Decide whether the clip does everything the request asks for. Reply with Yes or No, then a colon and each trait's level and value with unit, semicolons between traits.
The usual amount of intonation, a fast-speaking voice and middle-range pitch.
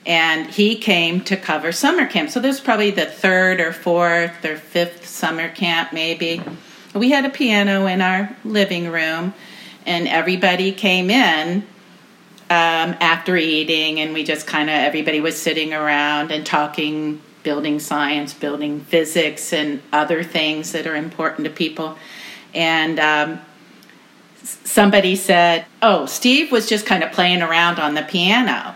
No: average, 3.5 semitones; average, 150 wpm; medium, 170 Hz